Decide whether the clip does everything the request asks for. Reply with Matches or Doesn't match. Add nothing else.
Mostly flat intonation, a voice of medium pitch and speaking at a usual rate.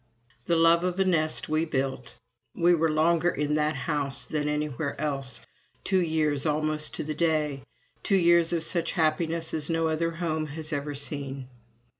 Matches